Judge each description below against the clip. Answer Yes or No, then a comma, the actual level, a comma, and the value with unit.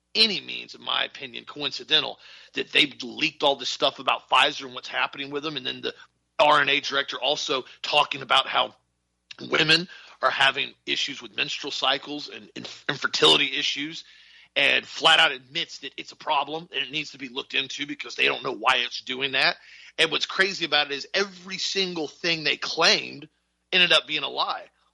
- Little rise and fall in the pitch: No, average, 3.5 semitones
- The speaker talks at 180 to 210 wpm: Yes, average, 190 wpm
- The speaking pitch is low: No, medium, 150 Hz